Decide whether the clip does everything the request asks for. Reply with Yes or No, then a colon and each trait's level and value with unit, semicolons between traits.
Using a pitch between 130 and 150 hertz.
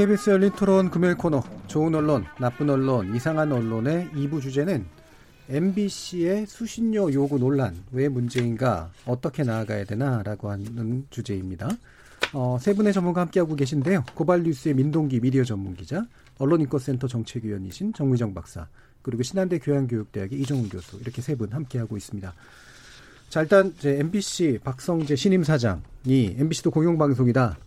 Yes: medium, 140 Hz